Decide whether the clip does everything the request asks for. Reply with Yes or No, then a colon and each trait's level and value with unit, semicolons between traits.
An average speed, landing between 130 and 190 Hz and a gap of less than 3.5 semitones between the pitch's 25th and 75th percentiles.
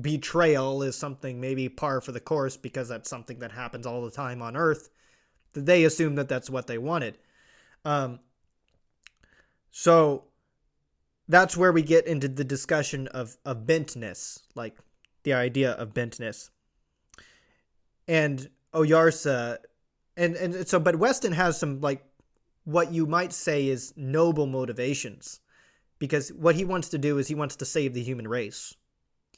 No: average, 150 wpm; medium, 140 Hz; average, 4.5 semitones